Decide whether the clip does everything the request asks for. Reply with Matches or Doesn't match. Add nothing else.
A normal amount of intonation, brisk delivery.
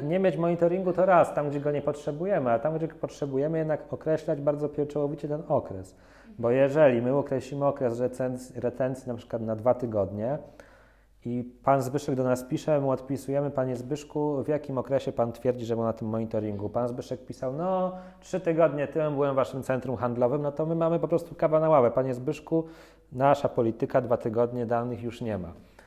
Matches